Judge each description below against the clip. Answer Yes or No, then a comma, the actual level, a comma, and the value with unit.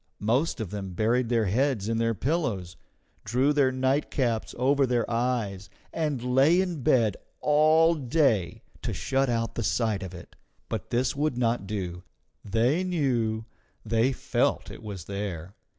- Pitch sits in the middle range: No, low, 120 Hz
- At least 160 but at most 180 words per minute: No, average, 150 wpm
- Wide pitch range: No, average, 4.6 semitones